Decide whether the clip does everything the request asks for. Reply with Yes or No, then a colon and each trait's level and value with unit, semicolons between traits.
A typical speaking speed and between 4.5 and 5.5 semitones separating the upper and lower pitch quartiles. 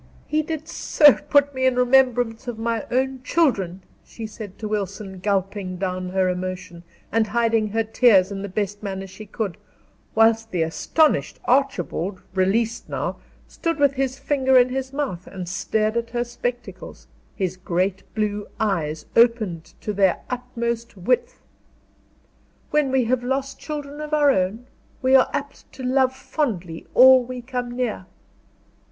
Yes: average, 155 wpm; average, 5.2 semitones